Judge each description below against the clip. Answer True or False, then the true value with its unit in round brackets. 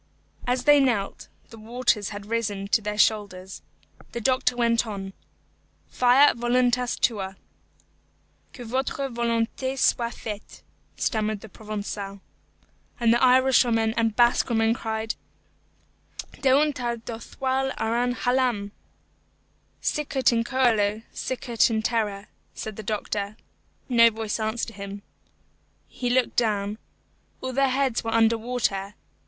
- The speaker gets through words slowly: True (125 wpm)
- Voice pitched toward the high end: True (230 Hz)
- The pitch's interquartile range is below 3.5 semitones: True (2.7 semitones)